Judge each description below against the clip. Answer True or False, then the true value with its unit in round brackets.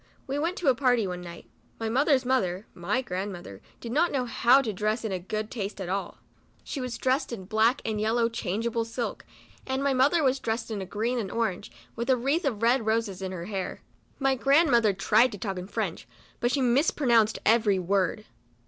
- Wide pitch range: False (4.3 semitones)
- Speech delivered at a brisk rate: True (210 wpm)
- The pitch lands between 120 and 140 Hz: False (230 Hz)